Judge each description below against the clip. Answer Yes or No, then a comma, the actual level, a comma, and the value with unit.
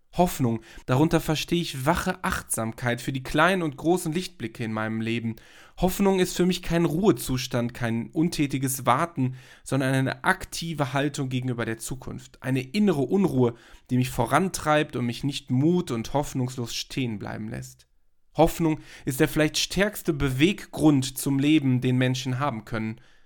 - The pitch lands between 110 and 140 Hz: Yes, low, 135 Hz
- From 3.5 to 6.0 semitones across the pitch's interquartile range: Yes, average, 5.0 semitones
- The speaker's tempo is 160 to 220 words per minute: No, average, 150 wpm